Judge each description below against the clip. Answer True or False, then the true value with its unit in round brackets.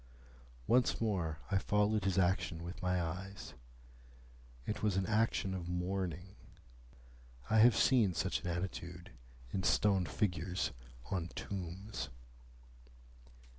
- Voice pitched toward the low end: True (95 Hz)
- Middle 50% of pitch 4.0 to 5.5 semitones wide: False (2.7 semitones)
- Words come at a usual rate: False (115 wpm)